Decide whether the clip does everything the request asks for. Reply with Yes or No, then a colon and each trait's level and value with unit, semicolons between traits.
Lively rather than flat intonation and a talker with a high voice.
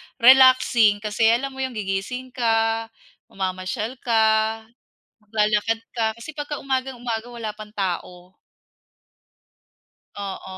No: average, 2.9 semitones; high, 225 Hz